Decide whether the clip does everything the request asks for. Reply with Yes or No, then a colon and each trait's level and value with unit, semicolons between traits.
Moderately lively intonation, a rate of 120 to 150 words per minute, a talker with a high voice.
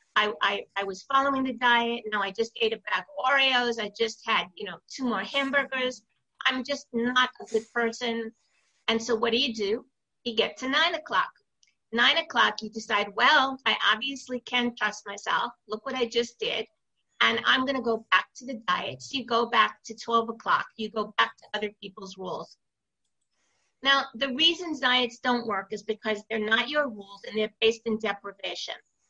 No: average, 3.2 semitones; average, 195 wpm; high, 235 Hz